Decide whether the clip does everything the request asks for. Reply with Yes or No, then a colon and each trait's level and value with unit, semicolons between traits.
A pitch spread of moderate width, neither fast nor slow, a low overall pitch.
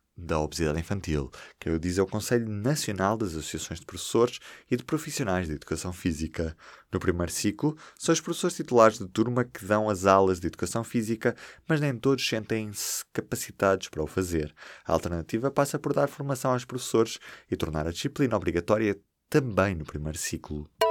No: wide, 6.7 semitones; average, 175 wpm; low, 105 Hz